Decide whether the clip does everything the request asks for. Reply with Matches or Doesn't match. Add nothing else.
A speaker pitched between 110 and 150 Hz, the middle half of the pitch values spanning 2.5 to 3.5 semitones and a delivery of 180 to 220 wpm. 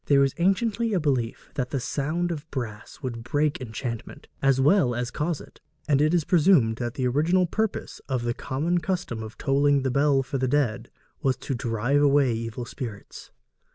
Doesn't match